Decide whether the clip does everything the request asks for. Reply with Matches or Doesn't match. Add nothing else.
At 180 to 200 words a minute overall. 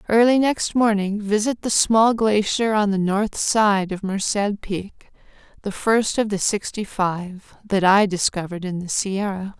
Doesn't match